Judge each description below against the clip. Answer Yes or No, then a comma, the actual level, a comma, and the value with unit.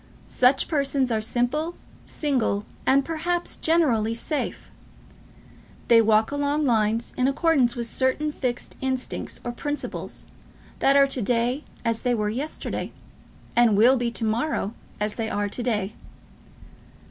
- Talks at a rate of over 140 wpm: No, slow, 135 wpm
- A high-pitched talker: Yes, very high, 250 Hz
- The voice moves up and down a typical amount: Yes, average, 3.9 semitones